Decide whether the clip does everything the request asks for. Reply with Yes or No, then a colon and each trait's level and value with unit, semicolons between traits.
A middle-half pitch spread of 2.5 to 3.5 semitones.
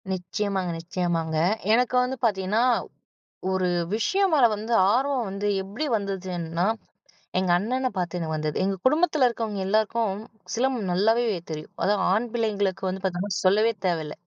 No: average, 4.2 semitones